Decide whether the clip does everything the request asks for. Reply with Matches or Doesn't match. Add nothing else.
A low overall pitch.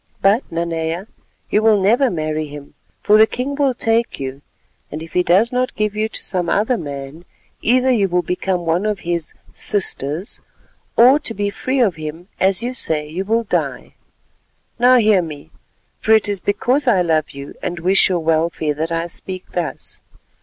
Doesn't match